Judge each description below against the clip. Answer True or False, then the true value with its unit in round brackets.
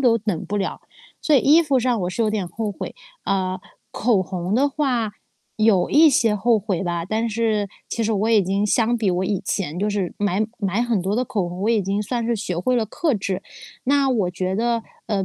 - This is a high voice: True (210 Hz)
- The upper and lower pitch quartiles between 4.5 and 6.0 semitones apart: False (3.5 semitones)